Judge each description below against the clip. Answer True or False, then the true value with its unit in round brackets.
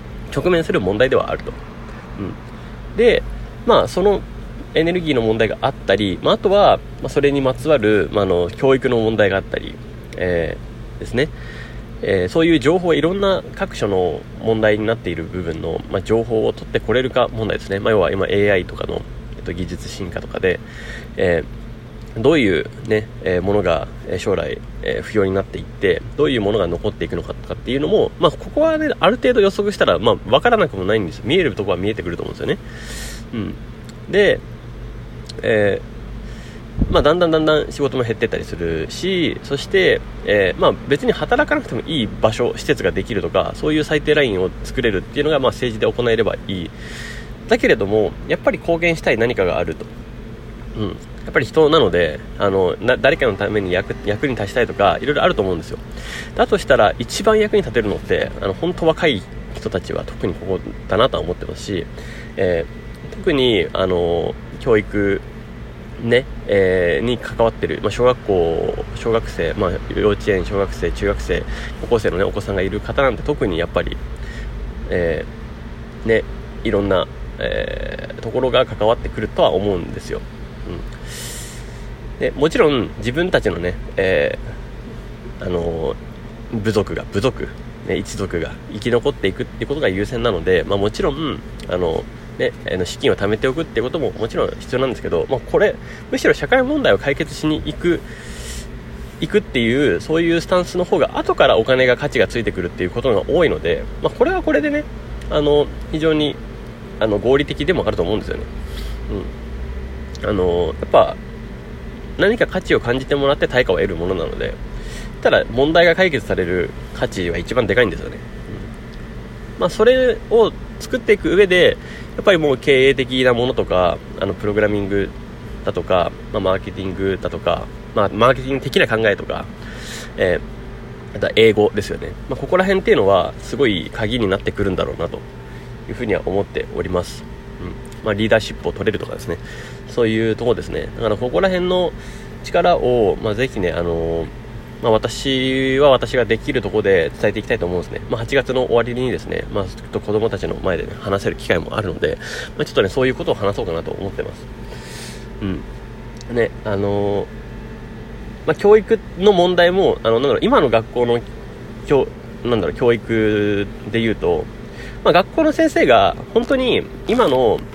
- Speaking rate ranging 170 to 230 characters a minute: False (355 characters per minute)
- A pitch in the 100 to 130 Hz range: True (120 Hz)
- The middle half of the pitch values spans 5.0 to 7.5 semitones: False (8.1 semitones)